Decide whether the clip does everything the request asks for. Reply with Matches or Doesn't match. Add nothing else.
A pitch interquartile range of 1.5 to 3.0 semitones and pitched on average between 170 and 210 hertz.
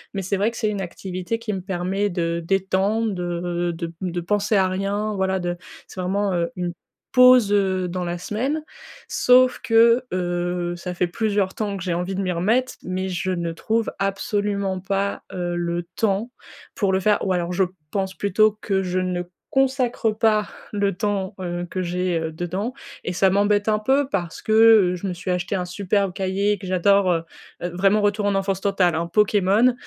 Matches